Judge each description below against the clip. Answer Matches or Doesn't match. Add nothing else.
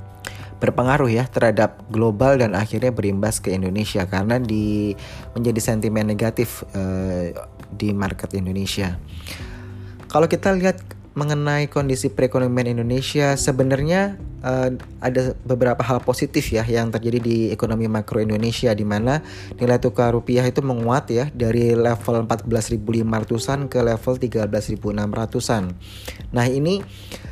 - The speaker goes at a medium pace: Matches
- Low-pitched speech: Matches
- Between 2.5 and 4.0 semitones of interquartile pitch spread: Matches